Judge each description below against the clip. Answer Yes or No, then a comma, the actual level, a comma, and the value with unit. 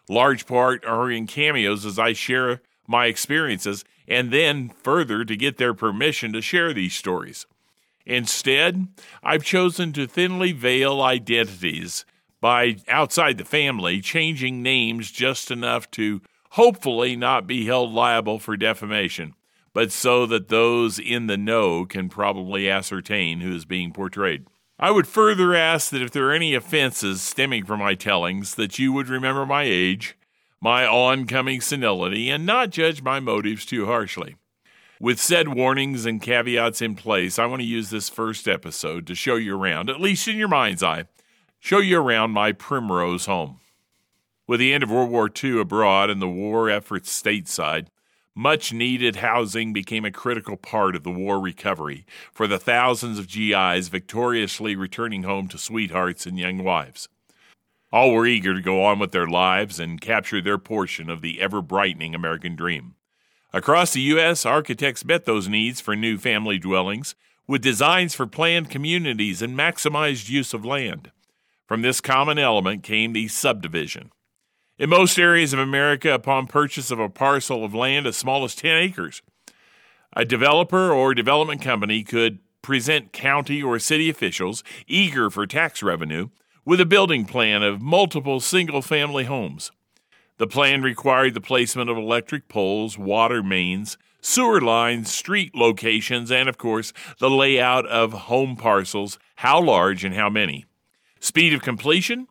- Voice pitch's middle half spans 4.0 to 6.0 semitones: Yes, average, 5.1 semitones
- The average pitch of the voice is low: Yes, low, 120 Hz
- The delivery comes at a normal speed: Yes, average, 160 wpm